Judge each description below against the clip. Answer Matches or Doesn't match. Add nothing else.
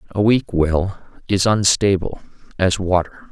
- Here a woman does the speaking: Doesn't match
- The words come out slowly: Matches